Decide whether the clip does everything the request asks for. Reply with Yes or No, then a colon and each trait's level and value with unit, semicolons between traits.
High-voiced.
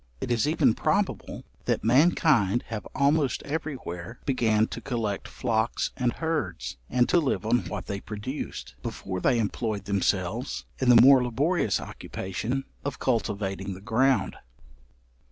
No: low, 115 Hz